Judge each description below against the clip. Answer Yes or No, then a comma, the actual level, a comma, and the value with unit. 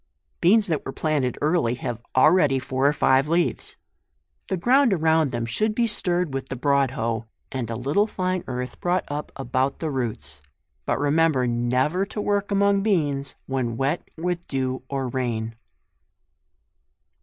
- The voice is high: No, medium, 140 Hz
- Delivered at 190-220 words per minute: No, average, 155 wpm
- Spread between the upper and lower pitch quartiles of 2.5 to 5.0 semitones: No, wide, 5.6 semitones